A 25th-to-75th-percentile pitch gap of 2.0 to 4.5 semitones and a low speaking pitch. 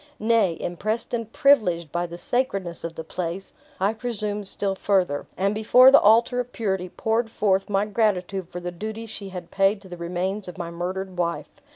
No: average, 3.6 semitones; high, 195 Hz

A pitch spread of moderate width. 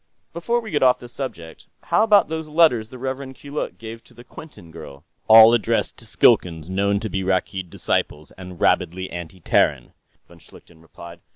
No: wide, 7.2 semitones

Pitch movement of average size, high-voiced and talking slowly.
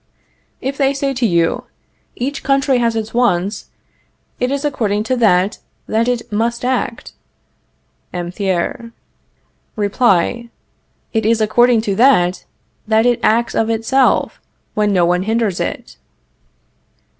Yes: average, 3.3 semitones; high, 225 Hz; slow, 130 wpm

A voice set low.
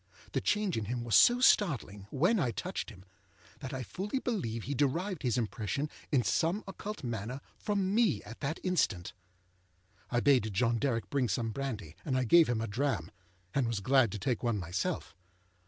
Yes: low, 125 Hz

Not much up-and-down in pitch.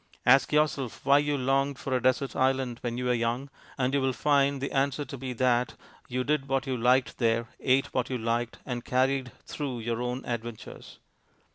Yes: narrow, 2.1 semitones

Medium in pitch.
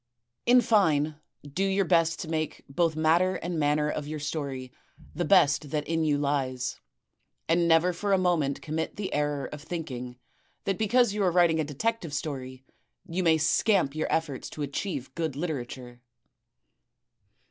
Yes: medium, 155 Hz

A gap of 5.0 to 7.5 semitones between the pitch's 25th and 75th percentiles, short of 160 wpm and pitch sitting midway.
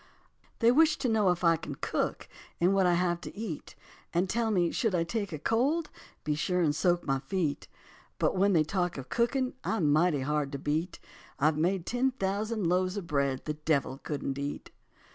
No: wide, 5.4 semitones; average, 200 wpm; medium, 175 Hz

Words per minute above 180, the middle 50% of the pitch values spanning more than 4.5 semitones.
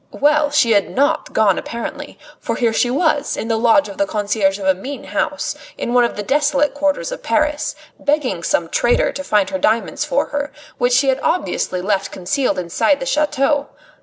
Yes: average, 195 wpm; wide, 5.6 semitones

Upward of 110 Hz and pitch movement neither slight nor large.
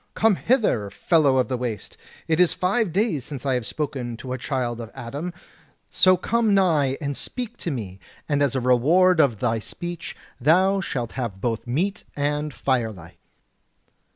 No: medium, 140 Hz; wide, 6.8 semitones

